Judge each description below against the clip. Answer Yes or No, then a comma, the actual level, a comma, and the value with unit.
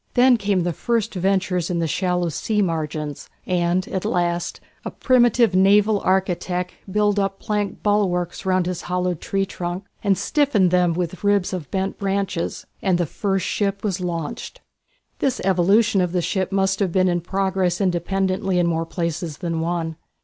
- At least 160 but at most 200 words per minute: Yes, average, 165 wpm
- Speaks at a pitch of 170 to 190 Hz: Yes, medium, 185 Hz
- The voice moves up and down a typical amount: No, narrow, 2.2 semitones